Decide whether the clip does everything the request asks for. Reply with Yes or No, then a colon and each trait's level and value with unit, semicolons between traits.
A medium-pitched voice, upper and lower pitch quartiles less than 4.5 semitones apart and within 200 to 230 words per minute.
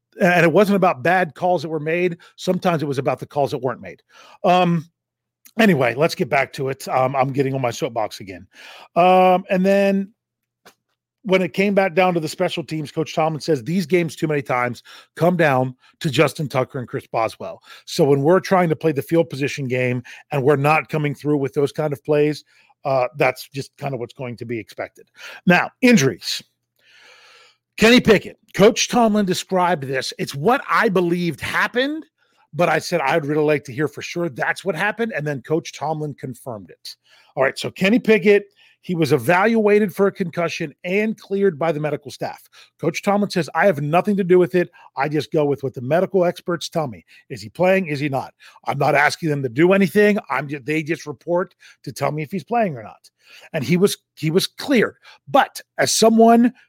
No: medium, 165 Hz; average, 4.9 semitones; fast, 205 wpm